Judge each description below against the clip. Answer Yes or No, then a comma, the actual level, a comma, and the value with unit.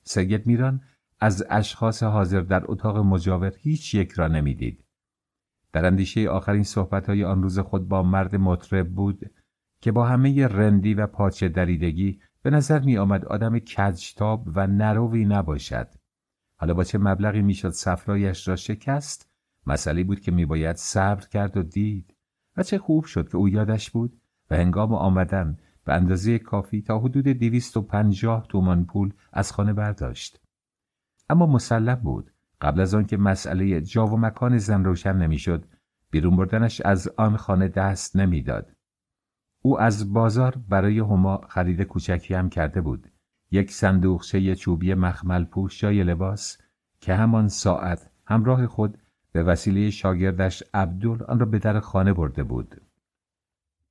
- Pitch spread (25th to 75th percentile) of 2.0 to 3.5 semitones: Yes, average, 2.8 semitones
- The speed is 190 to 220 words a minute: No, average, 145 wpm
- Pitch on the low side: Yes, low, 100 Hz